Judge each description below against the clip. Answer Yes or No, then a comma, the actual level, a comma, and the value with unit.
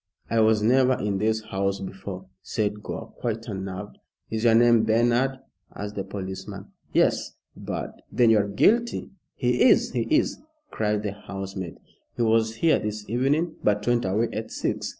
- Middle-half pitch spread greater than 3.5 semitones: No, average, 2.8 semitones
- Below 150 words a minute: No, average, 170 wpm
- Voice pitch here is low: Yes, low, 110 Hz